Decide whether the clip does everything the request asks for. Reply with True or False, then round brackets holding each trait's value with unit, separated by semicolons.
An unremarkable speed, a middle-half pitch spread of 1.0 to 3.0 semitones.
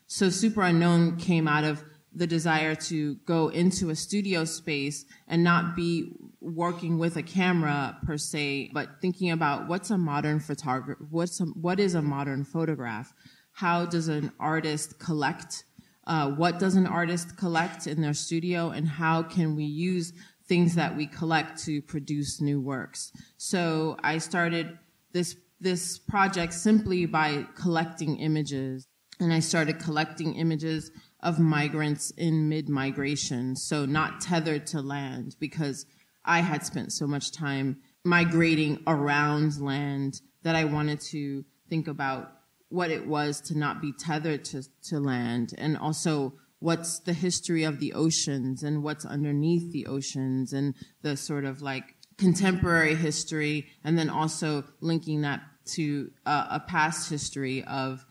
True (150 wpm; 2.7 semitones)